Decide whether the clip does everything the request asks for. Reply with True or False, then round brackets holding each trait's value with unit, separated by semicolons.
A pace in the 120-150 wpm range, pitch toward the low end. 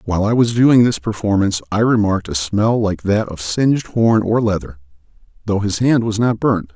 False (205 wpm; 105 Hz)